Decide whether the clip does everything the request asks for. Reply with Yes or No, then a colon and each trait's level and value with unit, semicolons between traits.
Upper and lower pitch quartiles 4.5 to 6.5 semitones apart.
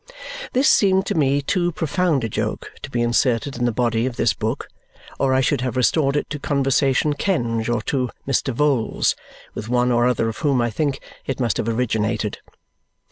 No: average, 3.4 semitones